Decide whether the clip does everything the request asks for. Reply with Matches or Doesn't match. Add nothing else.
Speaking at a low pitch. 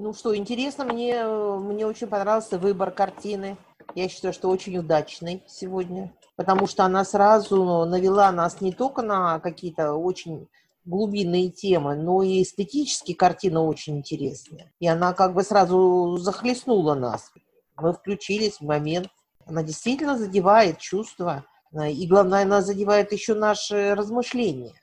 Doesn't match